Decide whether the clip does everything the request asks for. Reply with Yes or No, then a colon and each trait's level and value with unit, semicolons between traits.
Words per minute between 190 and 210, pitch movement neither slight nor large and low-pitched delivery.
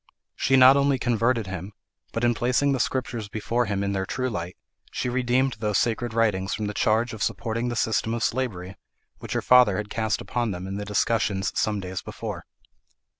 Yes: average, 195 wpm; average, 3.2 semitones; low, 115 Hz